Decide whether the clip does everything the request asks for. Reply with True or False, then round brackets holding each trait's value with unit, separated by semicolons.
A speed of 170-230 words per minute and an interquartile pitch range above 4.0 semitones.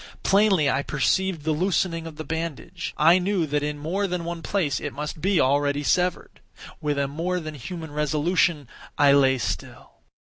False (175 wpm; 3.5 semitones)